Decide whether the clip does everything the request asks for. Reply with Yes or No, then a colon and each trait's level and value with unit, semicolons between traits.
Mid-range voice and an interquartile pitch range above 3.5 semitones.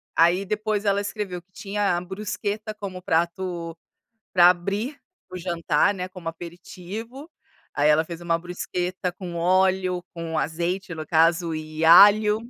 No: medium, 180 Hz; average, 3.0 semitones